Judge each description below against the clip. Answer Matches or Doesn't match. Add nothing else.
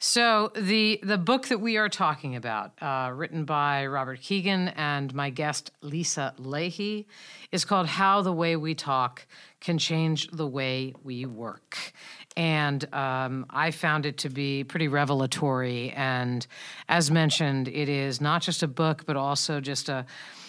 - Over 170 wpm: Doesn't match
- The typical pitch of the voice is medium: Matches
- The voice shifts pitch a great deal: Doesn't match